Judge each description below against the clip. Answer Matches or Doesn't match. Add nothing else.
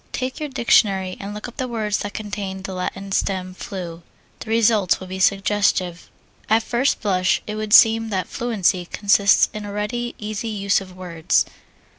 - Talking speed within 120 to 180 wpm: Matches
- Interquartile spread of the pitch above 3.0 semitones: Doesn't match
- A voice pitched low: Doesn't match